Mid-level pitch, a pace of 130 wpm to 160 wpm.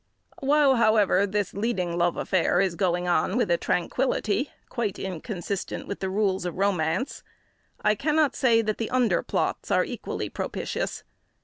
No: high, 200 Hz; average, 150 wpm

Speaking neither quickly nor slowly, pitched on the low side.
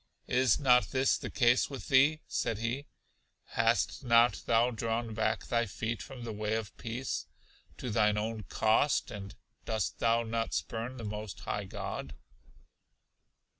Yes: average, 150 wpm; low, 115 Hz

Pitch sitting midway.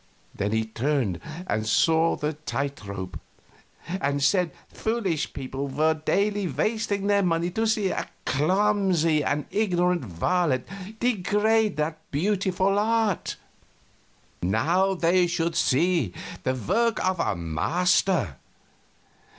Yes: medium, 170 Hz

